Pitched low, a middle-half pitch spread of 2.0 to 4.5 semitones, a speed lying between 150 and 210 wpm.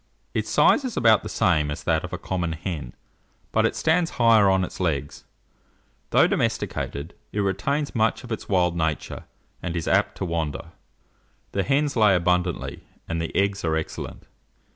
No: very low, 90 Hz; average, 5.0 semitones; average, 170 wpm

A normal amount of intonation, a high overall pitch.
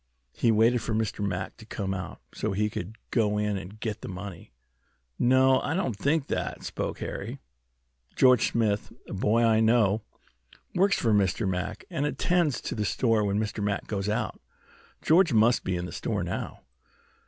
No: average, 3.3 semitones; low, 110 Hz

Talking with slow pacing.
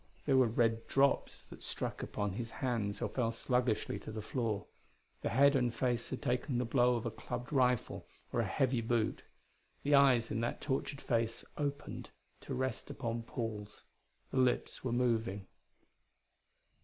No: average, 165 wpm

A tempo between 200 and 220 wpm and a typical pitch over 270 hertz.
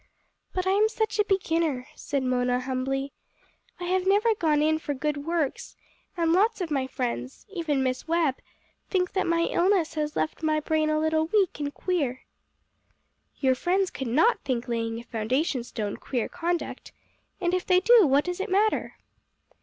No: average, 175 wpm; very high, 315 Hz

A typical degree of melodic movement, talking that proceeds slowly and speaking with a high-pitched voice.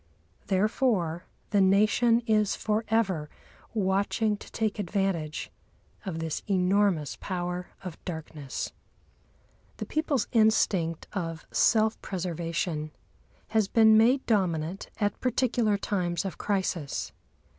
Yes: average, 4.1 semitones; slow, 105 wpm; high, 195 Hz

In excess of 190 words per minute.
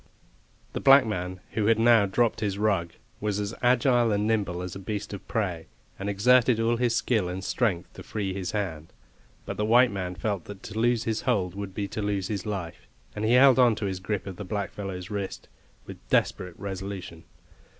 Yes: average, 200 wpm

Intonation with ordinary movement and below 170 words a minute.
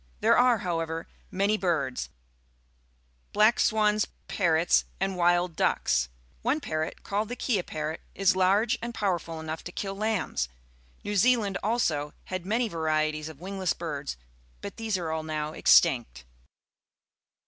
Yes: average, 5.0 semitones; slow, 135 wpm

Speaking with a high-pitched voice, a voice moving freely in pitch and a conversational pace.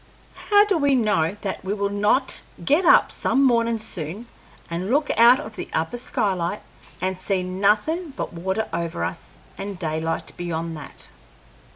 Yes: high, 200 Hz; wide, 6.0 semitones; average, 160 wpm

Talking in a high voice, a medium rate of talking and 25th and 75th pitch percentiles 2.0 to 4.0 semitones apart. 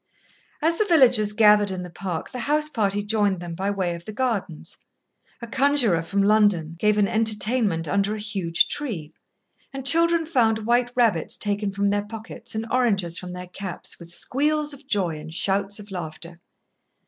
No: high, 205 Hz; average, 175 wpm; average, 4.9 semitones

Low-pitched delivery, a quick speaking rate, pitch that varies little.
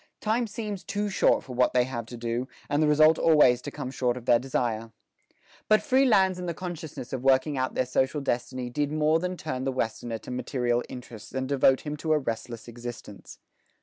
No: low, 130 Hz; fast, 210 wpm; average, 4.5 semitones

